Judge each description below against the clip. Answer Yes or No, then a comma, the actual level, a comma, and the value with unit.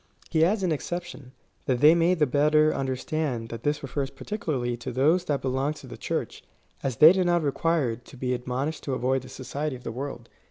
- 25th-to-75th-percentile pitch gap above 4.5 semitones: No, average, 3.7 semitones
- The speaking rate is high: Yes, fast, 210 wpm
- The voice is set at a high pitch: No, medium, 140 Hz